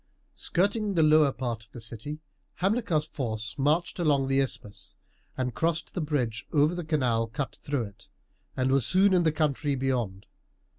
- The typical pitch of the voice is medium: Yes, medium, 145 Hz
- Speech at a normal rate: Yes, average, 165 wpm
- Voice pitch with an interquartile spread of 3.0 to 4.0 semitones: No, average, 4.7 semitones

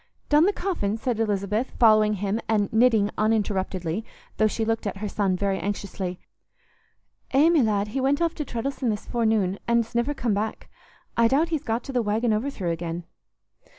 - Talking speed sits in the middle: Yes, average, 180 wpm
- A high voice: Yes, high, 220 Hz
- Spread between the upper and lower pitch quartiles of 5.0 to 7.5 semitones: No, average, 3.5 semitones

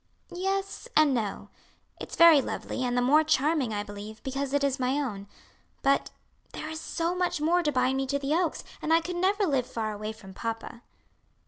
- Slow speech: No, average, 200 wpm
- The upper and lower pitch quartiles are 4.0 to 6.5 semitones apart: Yes, average, 5.2 semitones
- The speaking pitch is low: No, very high, 275 Hz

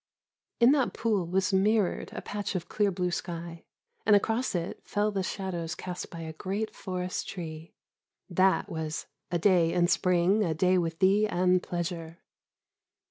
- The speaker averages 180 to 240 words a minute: No, average, 160 wpm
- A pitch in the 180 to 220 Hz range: Yes, medium, 185 Hz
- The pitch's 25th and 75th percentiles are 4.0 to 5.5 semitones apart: No, average, 2.8 semitones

